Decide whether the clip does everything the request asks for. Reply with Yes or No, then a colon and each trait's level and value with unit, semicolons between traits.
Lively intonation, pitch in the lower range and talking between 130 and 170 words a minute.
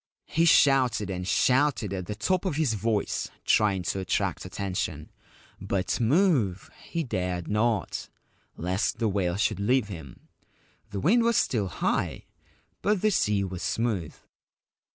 Yes: wide, 6.1 semitones; low, 105 Hz; average, 140 wpm